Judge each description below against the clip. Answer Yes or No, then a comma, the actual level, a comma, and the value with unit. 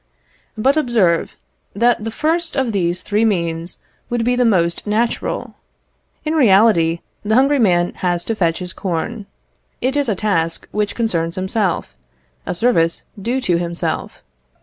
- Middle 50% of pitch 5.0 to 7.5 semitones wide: Yes, wide, 5.6 semitones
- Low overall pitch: No, high, 210 Hz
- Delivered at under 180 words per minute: Yes, average, 150 wpm